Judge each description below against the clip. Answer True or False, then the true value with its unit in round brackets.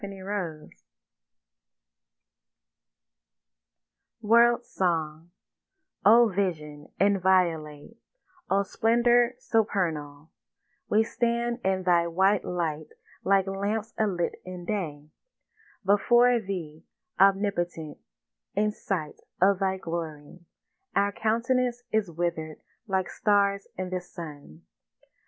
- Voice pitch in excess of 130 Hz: True (190 Hz)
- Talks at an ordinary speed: False (85 wpm)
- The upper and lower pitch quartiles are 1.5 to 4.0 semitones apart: False (4.4 semitones)